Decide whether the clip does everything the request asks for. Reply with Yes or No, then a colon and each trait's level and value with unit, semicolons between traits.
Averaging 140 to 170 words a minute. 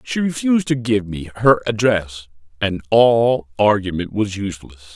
Yes: average, 145 wpm